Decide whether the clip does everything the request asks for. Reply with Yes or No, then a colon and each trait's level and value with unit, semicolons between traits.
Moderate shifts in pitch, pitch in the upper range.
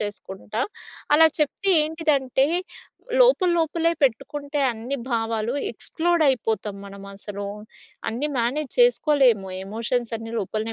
No: wide, 5.7 semitones; high, 245 Hz